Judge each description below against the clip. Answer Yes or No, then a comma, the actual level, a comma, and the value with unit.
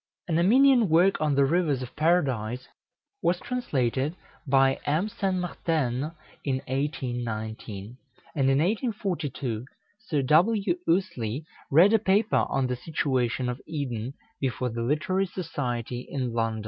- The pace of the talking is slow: Yes, slow, 130 wpm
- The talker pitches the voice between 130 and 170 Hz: Yes, medium, 140 Hz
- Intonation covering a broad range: Yes, wide, 6.1 semitones